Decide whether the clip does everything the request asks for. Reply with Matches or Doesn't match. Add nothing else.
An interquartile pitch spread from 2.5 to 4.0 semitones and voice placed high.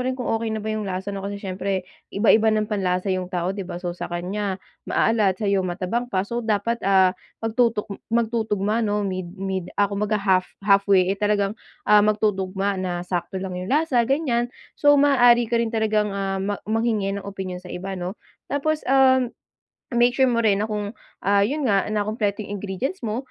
Matches